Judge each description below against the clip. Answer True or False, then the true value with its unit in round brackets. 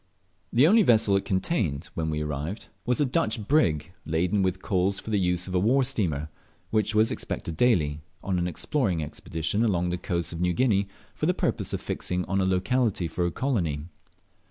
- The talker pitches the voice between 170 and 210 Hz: False (95 Hz)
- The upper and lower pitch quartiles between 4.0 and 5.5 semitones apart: True (4.7 semitones)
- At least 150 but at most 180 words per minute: False (195 wpm)